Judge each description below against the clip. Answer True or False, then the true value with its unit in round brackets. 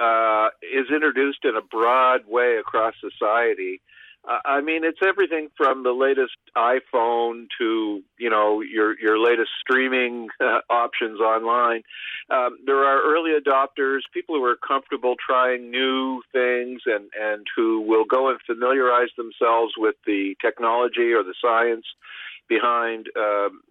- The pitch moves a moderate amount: True (3.3 semitones)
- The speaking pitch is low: True (125 Hz)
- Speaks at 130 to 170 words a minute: True (140 wpm)